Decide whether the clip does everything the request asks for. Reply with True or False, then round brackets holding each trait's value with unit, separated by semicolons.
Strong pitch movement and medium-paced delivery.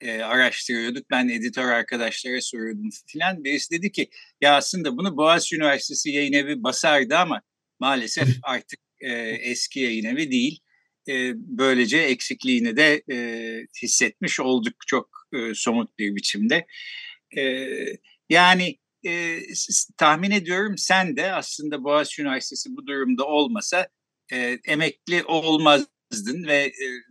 True (5.8 semitones; 125 wpm)